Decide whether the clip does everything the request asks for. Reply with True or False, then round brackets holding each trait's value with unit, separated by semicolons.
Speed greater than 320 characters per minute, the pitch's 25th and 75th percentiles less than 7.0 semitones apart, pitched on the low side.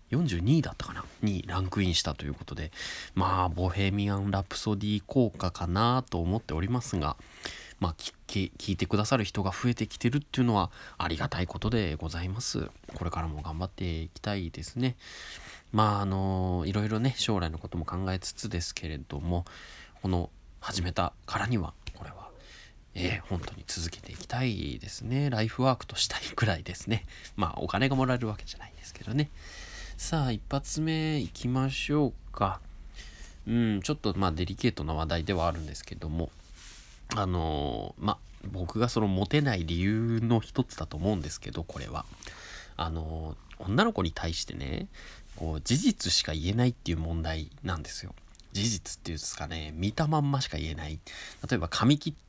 True (360 characters per minute; 5.6 semitones; 95 Hz)